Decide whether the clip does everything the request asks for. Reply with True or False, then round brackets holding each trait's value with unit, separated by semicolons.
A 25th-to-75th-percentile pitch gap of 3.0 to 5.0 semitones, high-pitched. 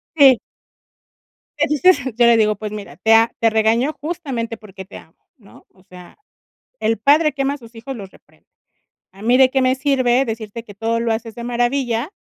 True (3.3 semitones; 230 Hz)